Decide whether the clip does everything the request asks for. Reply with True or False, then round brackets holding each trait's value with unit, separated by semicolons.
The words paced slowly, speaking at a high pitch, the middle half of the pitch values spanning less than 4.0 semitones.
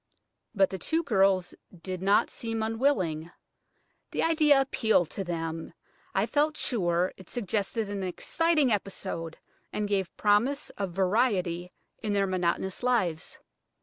False (130 wpm; 195 Hz; 4.6 semitones)